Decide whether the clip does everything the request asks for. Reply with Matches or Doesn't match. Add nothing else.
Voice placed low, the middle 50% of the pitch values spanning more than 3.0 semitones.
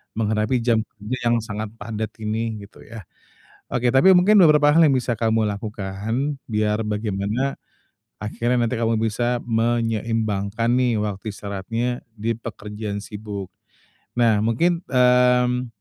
Doesn't match